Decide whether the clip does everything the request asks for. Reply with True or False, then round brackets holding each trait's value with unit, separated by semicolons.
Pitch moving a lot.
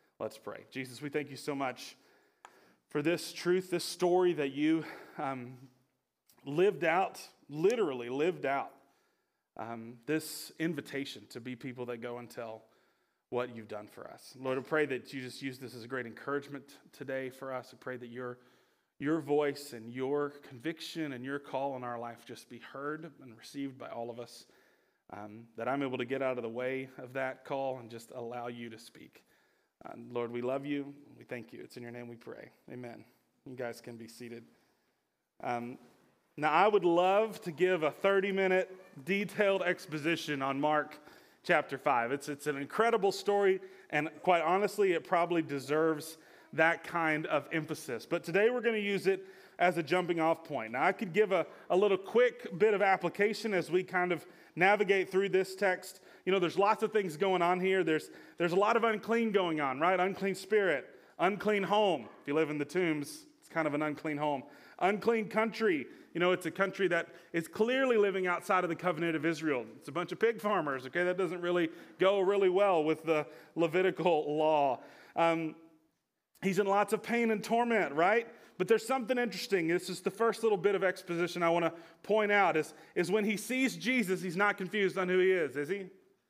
True (6.0 semitones)